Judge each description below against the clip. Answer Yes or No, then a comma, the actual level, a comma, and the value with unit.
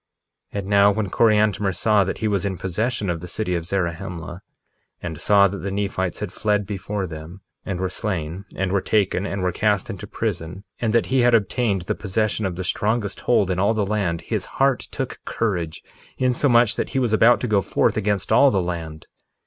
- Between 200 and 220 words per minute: Yes, fast, 205 wpm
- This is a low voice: Yes, low, 100 Hz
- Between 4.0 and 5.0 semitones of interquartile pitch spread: No, average, 2.9 semitones